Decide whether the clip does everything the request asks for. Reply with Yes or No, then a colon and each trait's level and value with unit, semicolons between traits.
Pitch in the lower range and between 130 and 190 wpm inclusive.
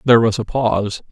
No: low, 110 Hz; fast, 215 wpm